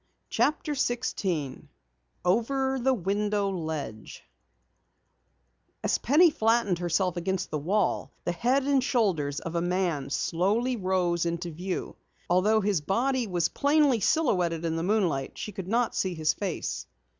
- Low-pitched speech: No, high, 190 Hz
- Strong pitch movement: Yes, wide, 5.8 semitones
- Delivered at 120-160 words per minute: Yes, slow, 135 wpm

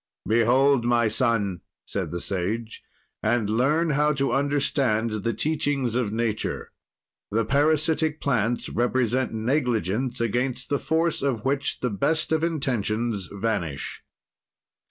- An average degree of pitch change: Yes, average, 4.2 semitones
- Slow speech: Yes, slow, 120 wpm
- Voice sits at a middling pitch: No, low, 120 Hz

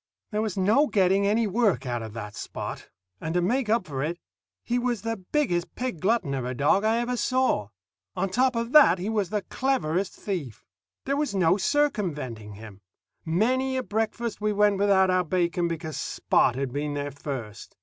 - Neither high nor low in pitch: No, high, 195 Hz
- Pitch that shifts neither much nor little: No, wide, 7.4 semitones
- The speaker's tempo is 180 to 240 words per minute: Yes, average, 190 wpm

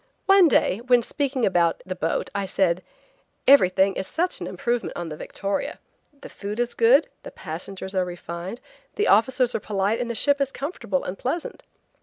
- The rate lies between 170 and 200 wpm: Yes, average, 180 wpm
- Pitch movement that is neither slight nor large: No, wide, 5.9 semitones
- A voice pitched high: Yes, high, 215 Hz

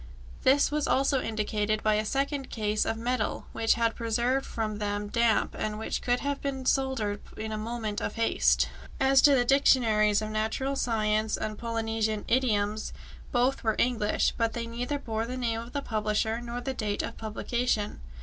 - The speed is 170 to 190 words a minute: Yes, average, 180 wpm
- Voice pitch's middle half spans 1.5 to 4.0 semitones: Yes, average, 2.8 semitones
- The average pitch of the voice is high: Yes, high, 230 Hz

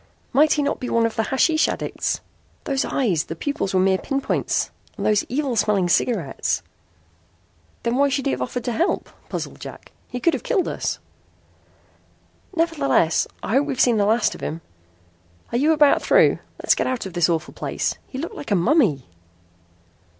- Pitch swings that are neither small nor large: No, wide, 6.7 semitones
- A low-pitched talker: No, high, 245 Hz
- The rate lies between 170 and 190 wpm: Yes, average, 180 wpm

